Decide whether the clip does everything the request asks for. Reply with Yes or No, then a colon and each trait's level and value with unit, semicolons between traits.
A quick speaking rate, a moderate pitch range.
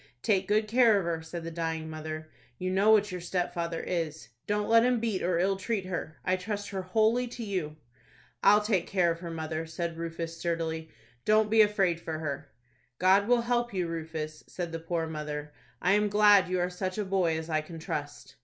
Yes: fast, 210 wpm; average, 4.1 semitones